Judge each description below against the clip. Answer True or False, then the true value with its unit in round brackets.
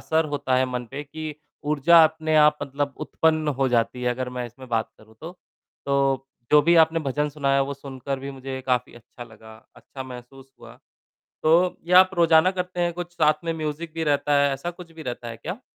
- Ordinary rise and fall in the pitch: True (3.5 semitones)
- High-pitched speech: False (145 Hz)